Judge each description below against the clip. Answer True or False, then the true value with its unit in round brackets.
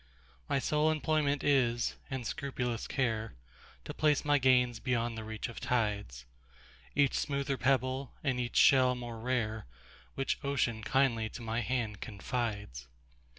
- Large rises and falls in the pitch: False (3.6 semitones)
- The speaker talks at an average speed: False (125 wpm)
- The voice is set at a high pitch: False (125 Hz)